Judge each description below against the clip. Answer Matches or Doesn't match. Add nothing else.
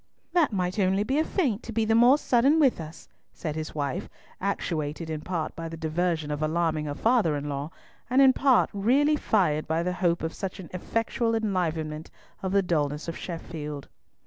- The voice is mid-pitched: Matches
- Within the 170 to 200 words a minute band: Matches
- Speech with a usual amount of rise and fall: Doesn't match